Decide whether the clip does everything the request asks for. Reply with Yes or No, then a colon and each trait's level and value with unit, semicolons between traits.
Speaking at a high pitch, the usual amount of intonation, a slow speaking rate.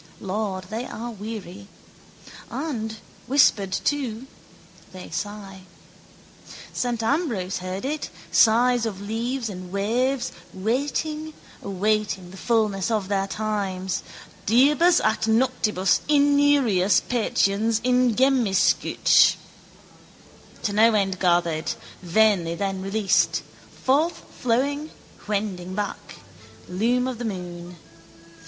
Yes: high, 215 Hz; average, 4.5 semitones; slow, 95 wpm